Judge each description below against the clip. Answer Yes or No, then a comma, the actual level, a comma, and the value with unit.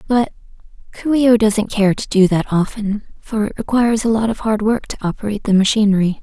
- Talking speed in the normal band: No, fast, 210 wpm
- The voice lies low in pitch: No, high, 215 Hz